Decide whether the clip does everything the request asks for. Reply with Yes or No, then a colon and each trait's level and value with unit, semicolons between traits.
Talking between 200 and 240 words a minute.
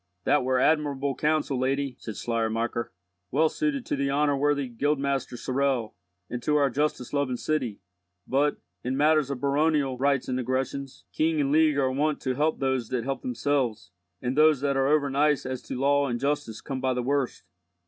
No: average, 185 wpm